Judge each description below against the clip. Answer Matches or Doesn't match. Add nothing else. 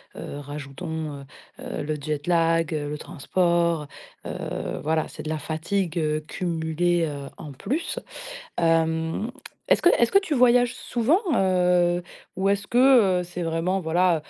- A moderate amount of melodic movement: Matches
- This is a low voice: Doesn't match